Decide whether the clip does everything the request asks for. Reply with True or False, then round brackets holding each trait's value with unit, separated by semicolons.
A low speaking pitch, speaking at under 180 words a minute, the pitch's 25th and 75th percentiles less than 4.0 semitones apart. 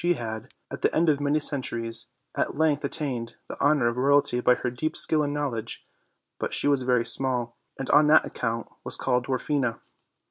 False (130 Hz; 190 wpm; 3.6 semitones)